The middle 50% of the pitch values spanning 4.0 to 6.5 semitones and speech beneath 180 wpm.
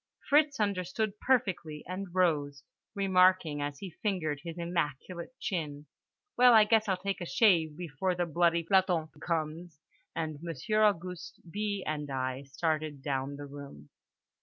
Yes: average, 4.4 semitones; slow, 135 wpm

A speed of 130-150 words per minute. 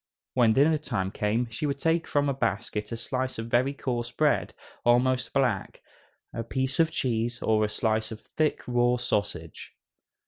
No: average, 170 wpm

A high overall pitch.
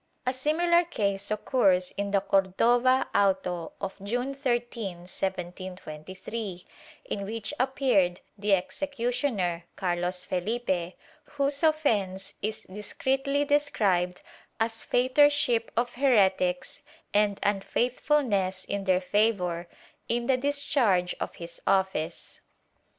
Yes: high, 205 Hz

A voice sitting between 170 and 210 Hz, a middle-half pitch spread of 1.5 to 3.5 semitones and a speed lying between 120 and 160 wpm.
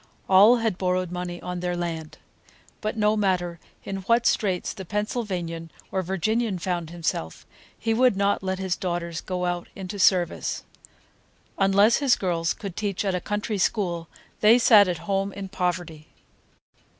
Yes: high, 190 Hz; average, 2.9 semitones; average, 150 wpm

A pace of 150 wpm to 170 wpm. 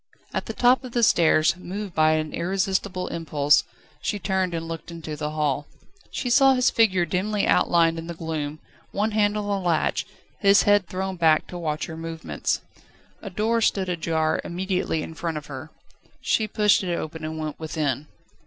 No: average, 180 wpm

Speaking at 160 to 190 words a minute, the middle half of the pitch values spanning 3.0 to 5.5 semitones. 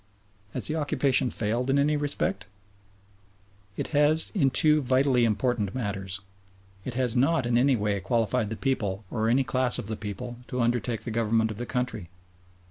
Yes: average, 170 wpm; average, 3.6 semitones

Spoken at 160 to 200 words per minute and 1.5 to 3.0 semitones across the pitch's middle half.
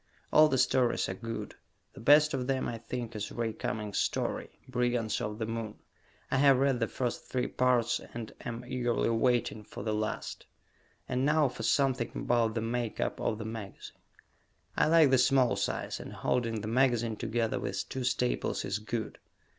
Yes: average, 180 wpm; narrow, 2.4 semitones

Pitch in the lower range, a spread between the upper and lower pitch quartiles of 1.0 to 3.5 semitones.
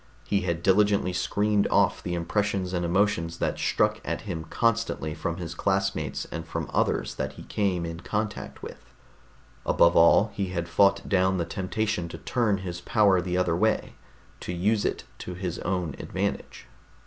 Yes: very low, 95 Hz; average, 3.1 semitones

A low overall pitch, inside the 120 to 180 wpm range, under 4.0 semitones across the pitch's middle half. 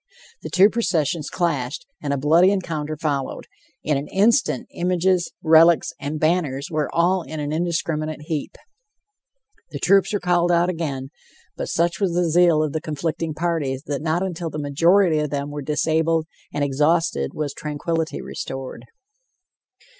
No: medium, 160 Hz; average, 155 wpm; average, 2.7 semitones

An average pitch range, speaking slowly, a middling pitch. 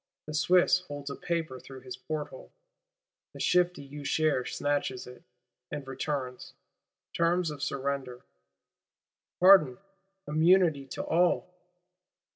Yes: average, 4.0 semitones; slow, 105 wpm; medium, 145 Hz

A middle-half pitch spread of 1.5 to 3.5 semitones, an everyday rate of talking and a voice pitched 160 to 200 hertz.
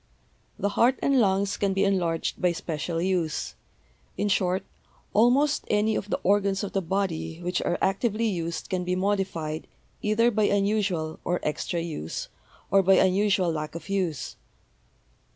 Yes: average, 3.1 semitones; average, 150 wpm; high, 190 Hz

